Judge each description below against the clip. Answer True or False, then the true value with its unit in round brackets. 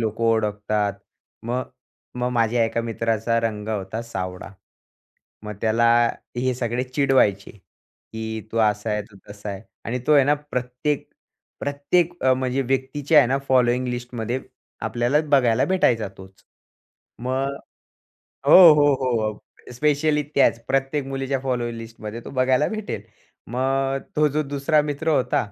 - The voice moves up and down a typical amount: True (3.5 semitones)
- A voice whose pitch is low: True (125 Hz)